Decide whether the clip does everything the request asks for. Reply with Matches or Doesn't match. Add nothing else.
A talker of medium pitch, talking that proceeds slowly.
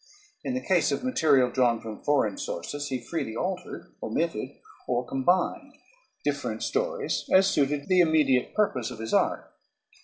Doesn't match